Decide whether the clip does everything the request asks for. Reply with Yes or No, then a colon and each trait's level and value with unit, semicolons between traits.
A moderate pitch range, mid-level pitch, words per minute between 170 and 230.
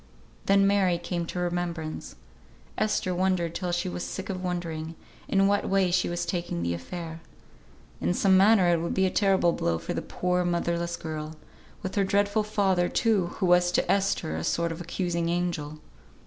No: narrow, 2.2 semitones; medium, 175 Hz; average, 180 wpm